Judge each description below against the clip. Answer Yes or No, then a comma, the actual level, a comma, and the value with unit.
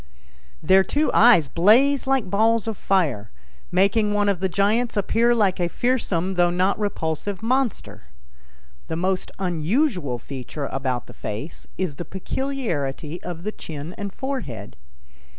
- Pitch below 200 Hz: Yes, high, 190 Hz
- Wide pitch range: Yes, wide, 5.7 semitones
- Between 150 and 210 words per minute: No, average, 140 wpm